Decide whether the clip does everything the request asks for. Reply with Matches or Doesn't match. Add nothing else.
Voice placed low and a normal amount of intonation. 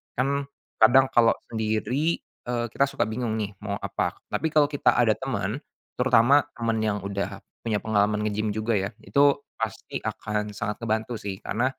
Matches